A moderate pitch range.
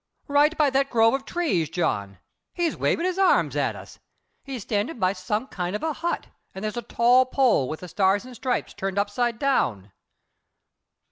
No: wide, 6.4 semitones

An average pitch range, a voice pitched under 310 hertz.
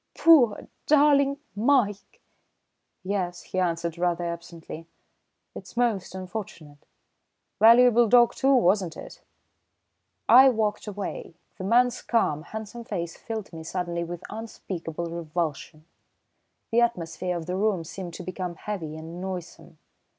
Yes: average, 4.9 semitones; medium, 185 Hz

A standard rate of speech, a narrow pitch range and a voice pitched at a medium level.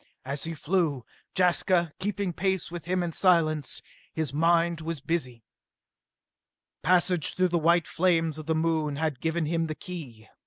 Yes: average, 155 wpm; narrow, 2.2 semitones; medium, 165 Hz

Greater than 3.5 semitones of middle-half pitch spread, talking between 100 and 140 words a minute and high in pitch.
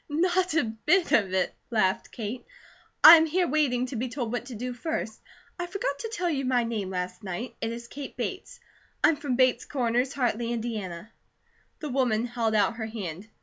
No: average, 4.7 semitones; average, 190 wpm; high, 245 Hz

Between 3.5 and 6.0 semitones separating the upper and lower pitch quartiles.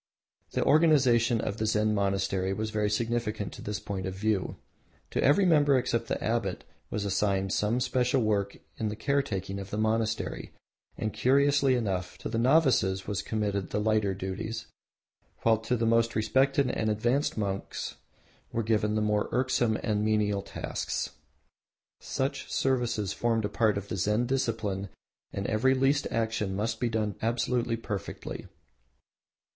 No: average, 2.9 semitones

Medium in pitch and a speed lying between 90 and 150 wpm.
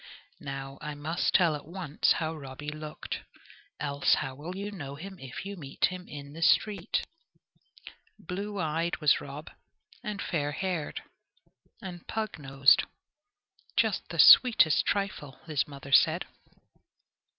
Yes: medium, 155 Hz; slow, 135 wpm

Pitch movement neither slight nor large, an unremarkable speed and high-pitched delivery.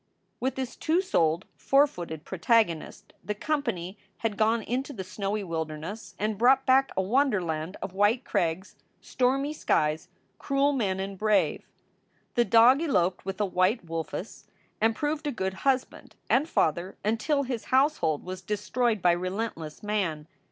No: wide, 6.3 semitones; average, 155 wpm; high, 210 Hz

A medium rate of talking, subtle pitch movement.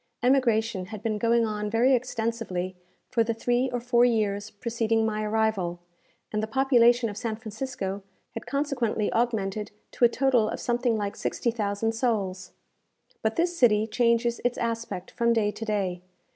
Yes: average, 160 wpm; narrow, 2.3 semitones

